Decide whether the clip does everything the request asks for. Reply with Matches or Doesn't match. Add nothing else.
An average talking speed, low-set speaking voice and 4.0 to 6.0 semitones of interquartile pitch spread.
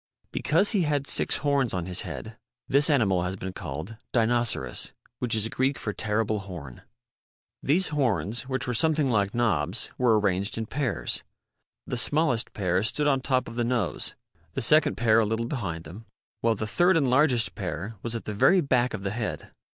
Matches